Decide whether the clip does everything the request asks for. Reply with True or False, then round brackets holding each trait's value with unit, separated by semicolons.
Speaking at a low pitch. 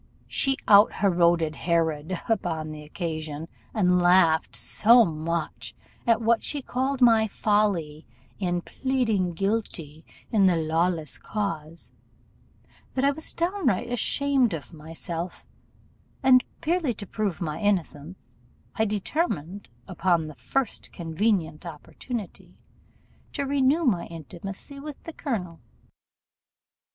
False (185 Hz)